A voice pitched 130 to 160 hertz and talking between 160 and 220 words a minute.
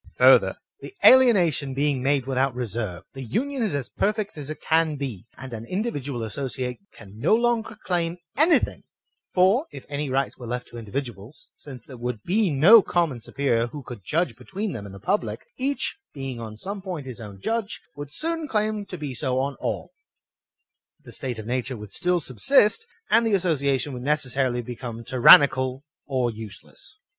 Yes: medium, 140 Hz; average, 180 wpm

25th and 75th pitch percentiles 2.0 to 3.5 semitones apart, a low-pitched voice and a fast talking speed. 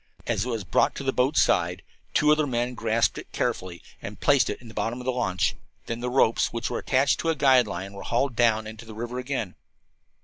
Yes: average, 3.0 semitones; low, 120 Hz; fast, 235 wpm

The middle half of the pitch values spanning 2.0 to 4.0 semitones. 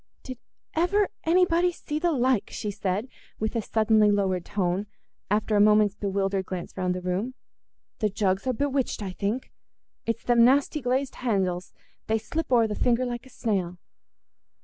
No: average, 4.7 semitones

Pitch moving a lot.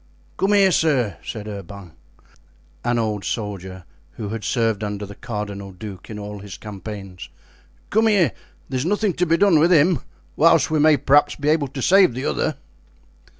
Yes: wide, 7.6 semitones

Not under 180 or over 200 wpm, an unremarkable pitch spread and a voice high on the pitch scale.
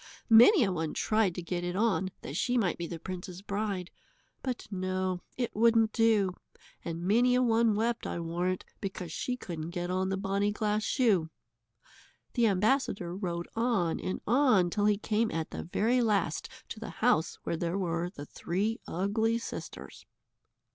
No: average, 170 wpm; average, 4.2 semitones; high, 195 Hz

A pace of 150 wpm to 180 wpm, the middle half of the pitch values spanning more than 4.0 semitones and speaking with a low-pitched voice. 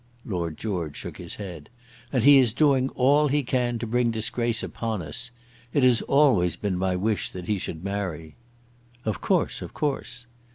Yes: average, 175 wpm; wide, 5.6 semitones; low, 110 Hz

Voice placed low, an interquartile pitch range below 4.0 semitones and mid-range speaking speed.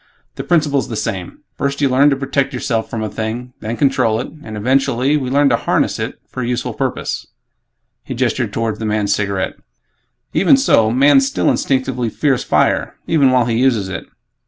Yes: low, 125 Hz; average, 3.6 semitones; average, 185 wpm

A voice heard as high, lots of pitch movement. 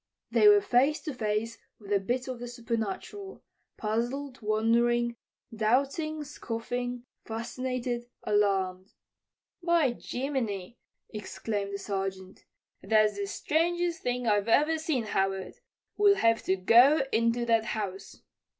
No: high, 235 Hz; average, 4.2 semitones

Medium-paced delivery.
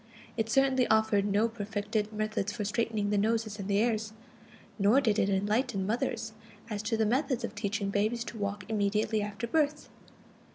Yes: average, 165 wpm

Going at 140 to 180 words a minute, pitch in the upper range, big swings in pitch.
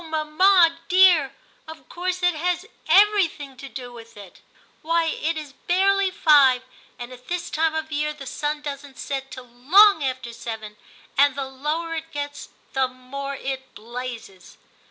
No: average, 160 wpm; very high, 290 Hz; average, 4.3 semitones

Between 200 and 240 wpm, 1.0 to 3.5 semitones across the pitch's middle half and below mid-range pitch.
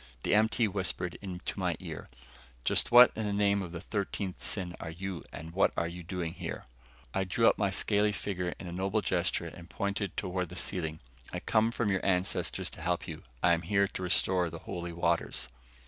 Yes: fast, 205 wpm; narrow, 2.6 semitones; very low, 95 Hz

